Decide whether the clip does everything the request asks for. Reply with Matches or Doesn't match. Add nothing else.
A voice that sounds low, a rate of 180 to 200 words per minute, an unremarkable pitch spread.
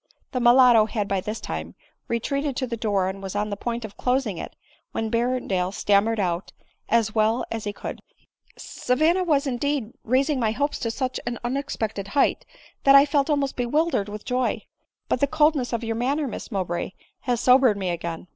Doesn't match